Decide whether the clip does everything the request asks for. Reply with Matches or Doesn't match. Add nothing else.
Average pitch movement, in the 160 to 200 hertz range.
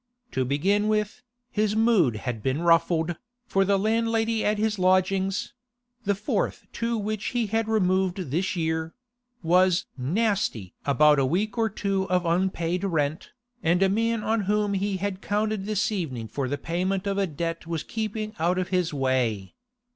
Matches